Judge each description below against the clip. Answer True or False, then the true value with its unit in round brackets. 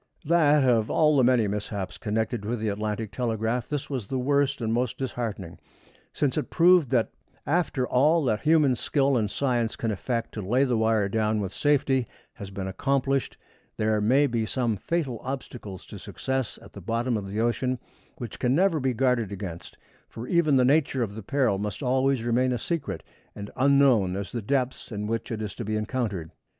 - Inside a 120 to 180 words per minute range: False (190 wpm)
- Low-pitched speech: True (120 Hz)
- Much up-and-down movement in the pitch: False (4.0 semitones)